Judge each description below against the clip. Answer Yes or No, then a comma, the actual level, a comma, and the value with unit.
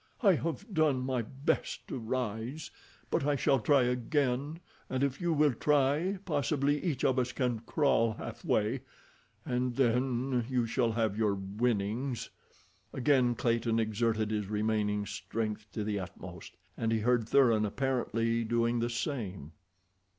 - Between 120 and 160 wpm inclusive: Yes, average, 145 wpm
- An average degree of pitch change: Yes, average, 3.6 semitones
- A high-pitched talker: No, low, 120 Hz